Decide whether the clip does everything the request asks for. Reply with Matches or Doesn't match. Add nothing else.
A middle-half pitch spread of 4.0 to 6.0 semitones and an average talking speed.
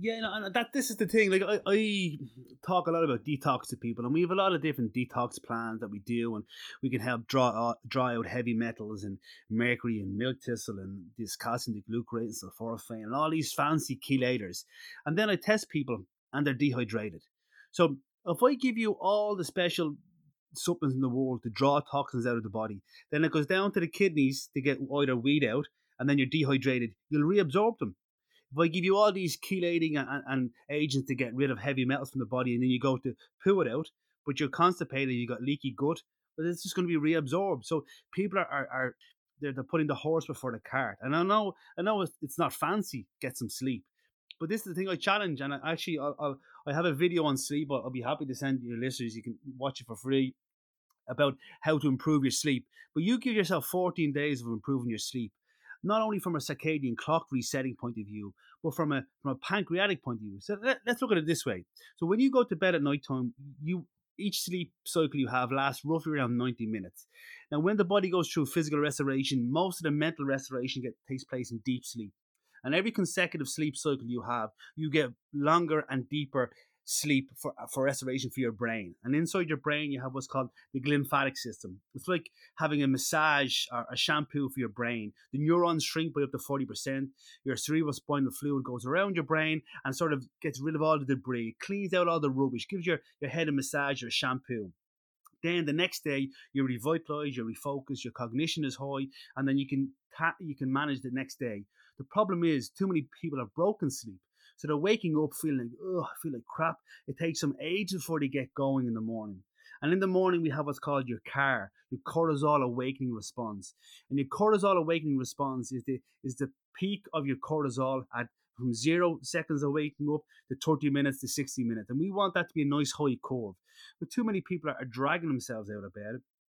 Doesn't match